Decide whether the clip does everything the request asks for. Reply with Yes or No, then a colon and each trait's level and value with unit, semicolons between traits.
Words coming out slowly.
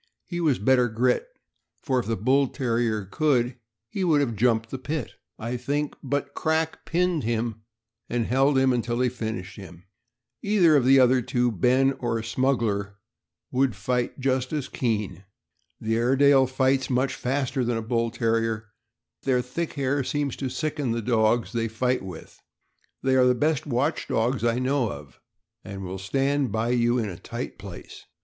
No: average, 170 wpm